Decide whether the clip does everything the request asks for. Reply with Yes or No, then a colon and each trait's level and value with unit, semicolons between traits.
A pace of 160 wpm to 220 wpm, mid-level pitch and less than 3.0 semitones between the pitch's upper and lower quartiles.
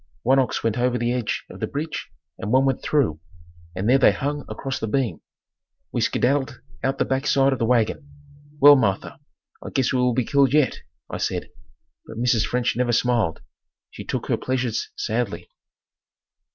No: average, 180 wpm; low, 125 Hz; narrow, 2.4 semitones